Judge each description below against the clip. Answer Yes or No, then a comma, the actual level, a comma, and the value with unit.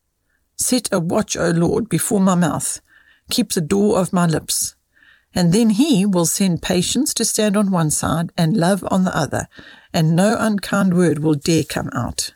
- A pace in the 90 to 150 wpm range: No, average, 185 wpm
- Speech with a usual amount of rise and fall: Yes, average, 4.0 semitones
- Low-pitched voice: No, medium, 185 Hz